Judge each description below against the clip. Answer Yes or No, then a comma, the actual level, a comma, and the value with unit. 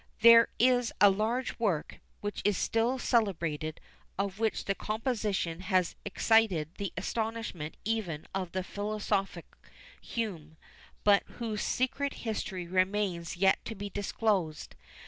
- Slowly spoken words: Yes, slow, 125 wpm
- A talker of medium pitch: No, high, 205 Hz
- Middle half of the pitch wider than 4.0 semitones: No, average, 3.6 semitones